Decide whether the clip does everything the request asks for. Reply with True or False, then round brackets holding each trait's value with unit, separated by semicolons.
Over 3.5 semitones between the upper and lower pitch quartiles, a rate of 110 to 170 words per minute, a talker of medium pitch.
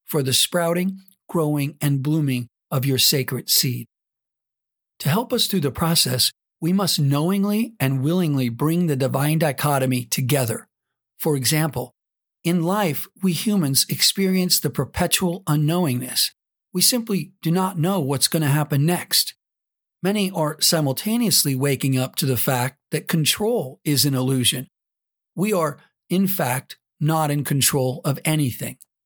True (4.8 semitones; 140 wpm; 150 Hz)